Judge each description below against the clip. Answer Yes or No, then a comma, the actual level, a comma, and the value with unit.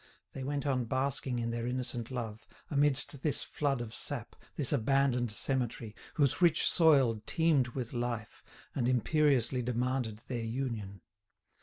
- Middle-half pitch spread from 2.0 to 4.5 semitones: Yes, average, 2.9 semitones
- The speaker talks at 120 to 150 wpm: Yes, average, 140 wpm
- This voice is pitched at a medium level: No, low, 125 Hz